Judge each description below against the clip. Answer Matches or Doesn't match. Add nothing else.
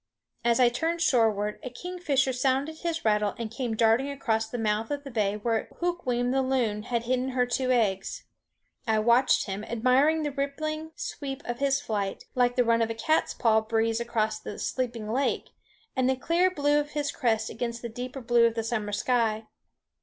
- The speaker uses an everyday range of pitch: Matches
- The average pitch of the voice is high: Matches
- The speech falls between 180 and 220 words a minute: Matches